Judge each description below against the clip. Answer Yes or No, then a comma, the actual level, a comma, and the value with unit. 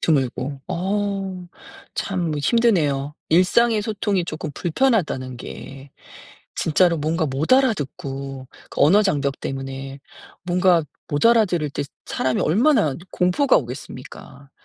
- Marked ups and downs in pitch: Yes, wide, 6.4 semitones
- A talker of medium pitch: Yes, medium, 165 Hz